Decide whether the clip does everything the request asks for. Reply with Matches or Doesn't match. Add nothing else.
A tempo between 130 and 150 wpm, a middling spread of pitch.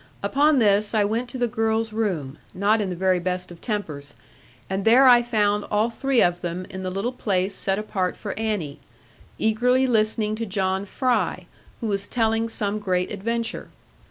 Doesn't match